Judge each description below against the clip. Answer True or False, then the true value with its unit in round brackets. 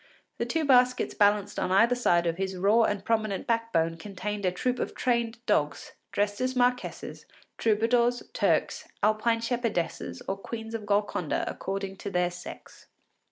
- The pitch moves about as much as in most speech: True (3.6 semitones)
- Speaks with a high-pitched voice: True (210 Hz)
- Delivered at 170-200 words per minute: False (155 wpm)